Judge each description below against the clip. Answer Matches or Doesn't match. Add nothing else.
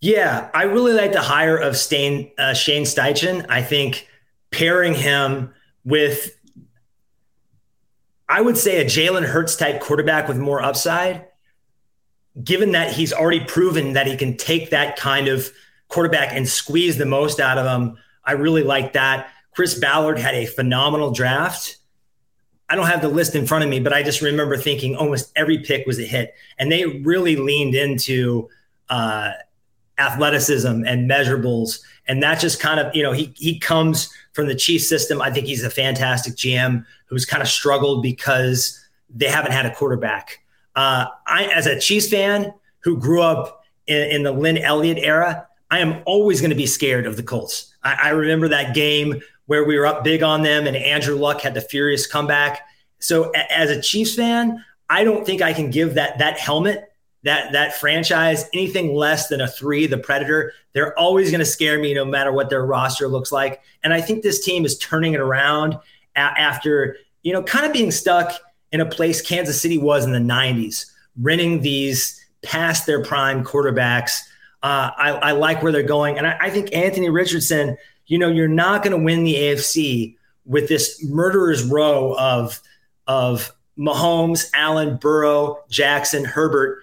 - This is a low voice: Doesn't match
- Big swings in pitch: Doesn't match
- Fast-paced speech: Doesn't match